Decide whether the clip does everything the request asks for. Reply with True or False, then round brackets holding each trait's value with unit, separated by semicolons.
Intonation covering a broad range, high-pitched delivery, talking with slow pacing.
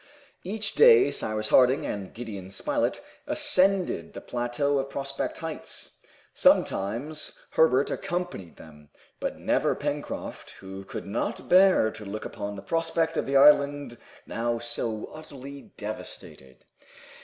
False (6.9 semitones; 135 Hz; 125 wpm)